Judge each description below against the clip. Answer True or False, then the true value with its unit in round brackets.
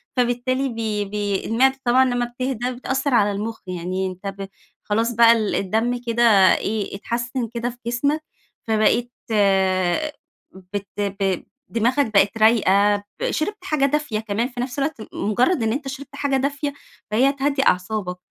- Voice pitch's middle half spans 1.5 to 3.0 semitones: False (4.3 semitones)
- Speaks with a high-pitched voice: True (235 Hz)